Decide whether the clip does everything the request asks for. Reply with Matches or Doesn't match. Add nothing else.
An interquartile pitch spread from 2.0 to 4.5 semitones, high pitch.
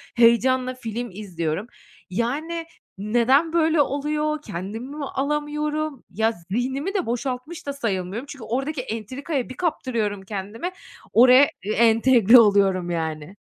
Doesn't match